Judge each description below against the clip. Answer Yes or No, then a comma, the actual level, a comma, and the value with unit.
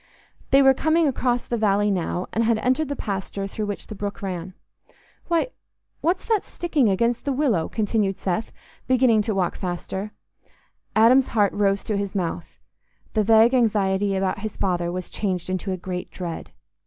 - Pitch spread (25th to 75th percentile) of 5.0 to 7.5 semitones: No, average, 4.1 semitones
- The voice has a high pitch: Yes, high, 210 Hz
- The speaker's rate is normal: Yes, average, 170 wpm